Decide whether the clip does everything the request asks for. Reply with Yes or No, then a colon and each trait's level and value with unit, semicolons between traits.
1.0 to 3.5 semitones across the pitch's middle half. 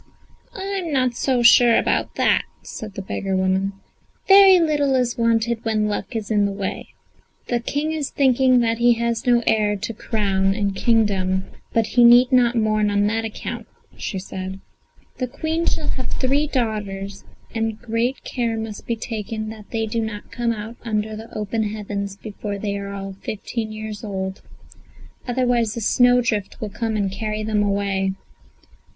Yes: average, 2.8 semitones